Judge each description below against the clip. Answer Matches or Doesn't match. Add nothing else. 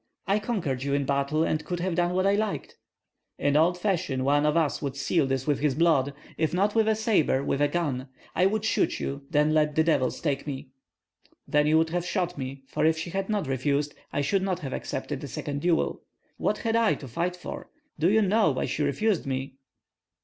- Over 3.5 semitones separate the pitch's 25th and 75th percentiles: Matches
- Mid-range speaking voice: Matches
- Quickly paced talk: Matches